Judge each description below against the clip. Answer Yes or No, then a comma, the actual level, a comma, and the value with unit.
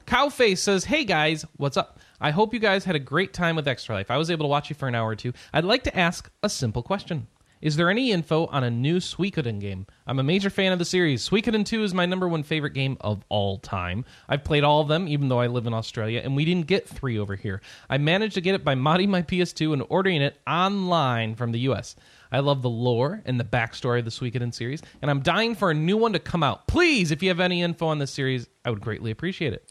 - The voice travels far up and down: Yes, wide, 6.6 semitones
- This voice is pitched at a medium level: Yes, medium, 155 Hz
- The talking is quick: Yes, fast, 265 wpm